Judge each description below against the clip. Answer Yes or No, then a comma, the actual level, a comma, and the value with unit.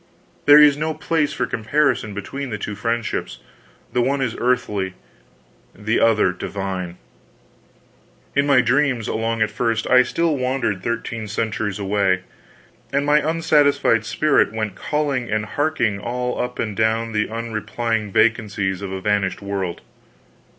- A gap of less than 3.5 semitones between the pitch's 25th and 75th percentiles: No, average, 4.6 semitones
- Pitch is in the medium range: No, low, 115 Hz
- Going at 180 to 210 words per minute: No, average, 140 wpm